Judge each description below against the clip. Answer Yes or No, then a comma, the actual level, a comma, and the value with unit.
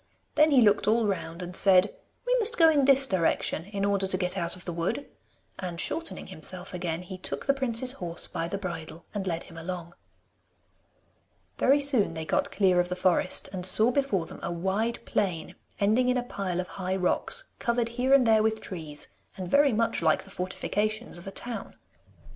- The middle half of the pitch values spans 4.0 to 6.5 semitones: Yes, average, 5.3 semitones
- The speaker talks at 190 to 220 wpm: Yes, average, 200 wpm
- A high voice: Yes, high, 195 Hz